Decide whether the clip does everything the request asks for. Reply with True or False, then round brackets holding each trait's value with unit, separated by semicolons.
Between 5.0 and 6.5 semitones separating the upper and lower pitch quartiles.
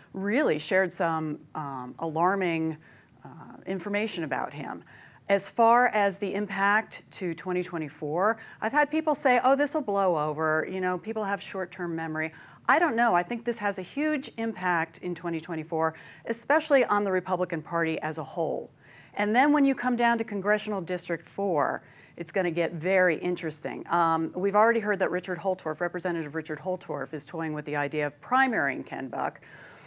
False (4.6 semitones)